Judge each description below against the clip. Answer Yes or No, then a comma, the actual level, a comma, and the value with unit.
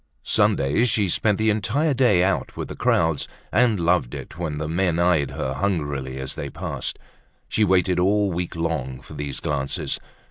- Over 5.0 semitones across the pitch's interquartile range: Yes, wide, 5.6 semitones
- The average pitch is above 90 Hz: No, very low, 85 Hz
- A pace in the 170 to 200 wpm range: Yes, average, 175 wpm